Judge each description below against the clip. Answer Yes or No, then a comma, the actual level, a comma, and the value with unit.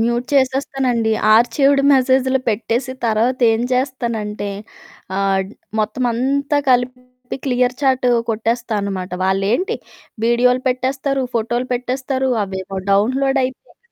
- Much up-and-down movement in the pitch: No, average, 2.7 semitones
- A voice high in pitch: Yes, very high, 250 Hz